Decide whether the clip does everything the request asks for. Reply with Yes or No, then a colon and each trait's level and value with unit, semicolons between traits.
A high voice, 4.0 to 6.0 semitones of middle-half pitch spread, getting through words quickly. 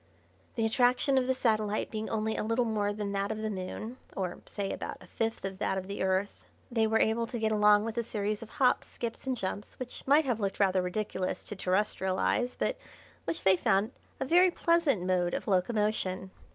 No: high, 215 Hz; average, 3.3 semitones; fast, 210 wpm